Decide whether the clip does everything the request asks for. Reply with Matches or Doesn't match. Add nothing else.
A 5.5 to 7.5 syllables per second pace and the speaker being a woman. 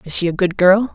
Matches